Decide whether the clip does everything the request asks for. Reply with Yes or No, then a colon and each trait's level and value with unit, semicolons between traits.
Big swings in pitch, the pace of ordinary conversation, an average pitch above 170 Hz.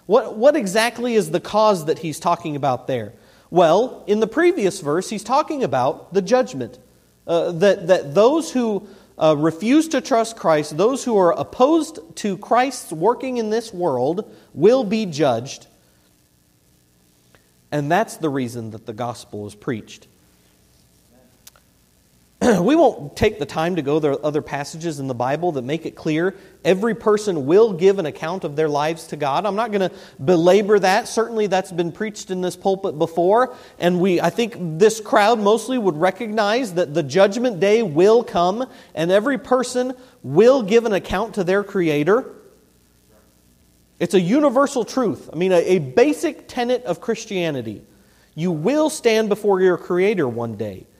Yes: wide, 6.8 semitones; average, 165 wpm; medium, 185 Hz